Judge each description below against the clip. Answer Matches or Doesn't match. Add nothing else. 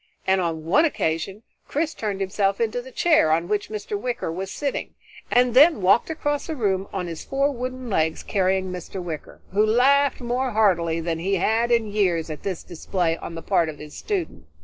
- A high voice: Matches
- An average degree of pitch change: Doesn't match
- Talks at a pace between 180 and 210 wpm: Matches